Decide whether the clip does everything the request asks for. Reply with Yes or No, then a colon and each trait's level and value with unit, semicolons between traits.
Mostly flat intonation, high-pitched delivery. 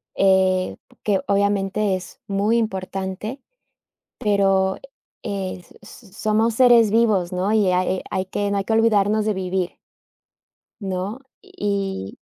Yes: narrow, 2.1 semitones; high, 200 Hz